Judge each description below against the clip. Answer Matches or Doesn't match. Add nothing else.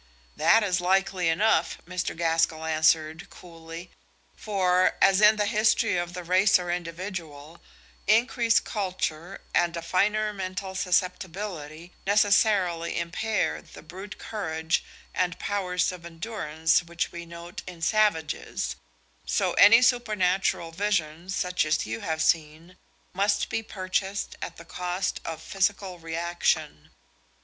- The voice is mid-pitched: Matches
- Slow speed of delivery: Matches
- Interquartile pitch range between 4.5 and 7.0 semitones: Doesn't match